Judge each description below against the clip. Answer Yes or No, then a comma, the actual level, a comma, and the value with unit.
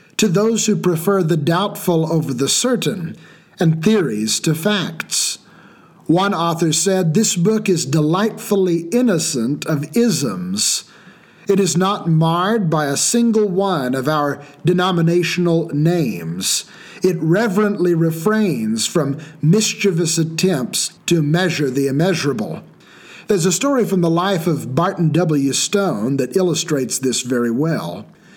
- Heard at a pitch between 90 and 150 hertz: No, medium, 175 Hz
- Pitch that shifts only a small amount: No, average, 4.1 semitones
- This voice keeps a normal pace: No, slow, 125 wpm